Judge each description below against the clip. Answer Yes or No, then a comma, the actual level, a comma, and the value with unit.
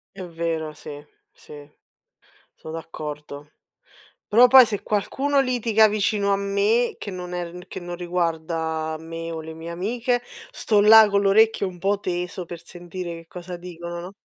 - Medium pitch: Yes, medium, 180 Hz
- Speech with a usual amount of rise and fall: Yes, average, 3.7 semitones